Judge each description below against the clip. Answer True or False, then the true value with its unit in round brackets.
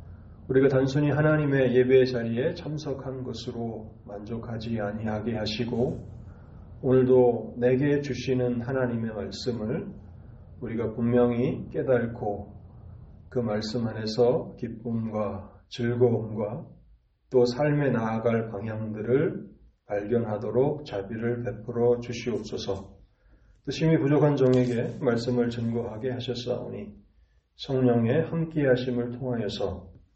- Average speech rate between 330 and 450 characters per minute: False (255 characters per minute)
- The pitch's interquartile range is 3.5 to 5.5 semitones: False (3.1 semitones)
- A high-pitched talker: False (120 Hz)